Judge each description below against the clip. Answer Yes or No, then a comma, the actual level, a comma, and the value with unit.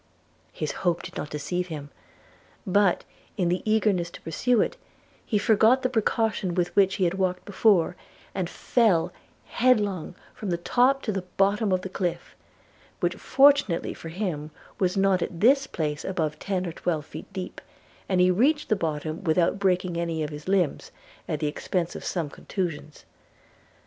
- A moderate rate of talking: Yes, average, 170 wpm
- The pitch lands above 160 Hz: Yes, medium, 185 Hz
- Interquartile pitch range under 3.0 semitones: No, average, 3.6 semitones